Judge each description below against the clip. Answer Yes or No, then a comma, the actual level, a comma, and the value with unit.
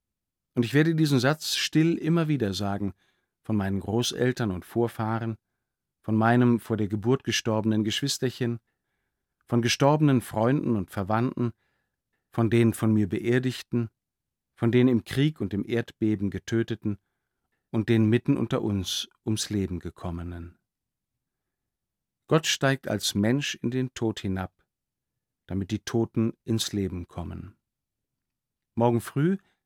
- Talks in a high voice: No, low, 115 Hz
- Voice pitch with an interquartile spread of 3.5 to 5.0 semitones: No, average, 3.0 semitones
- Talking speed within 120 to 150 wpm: Yes, slow, 125 wpm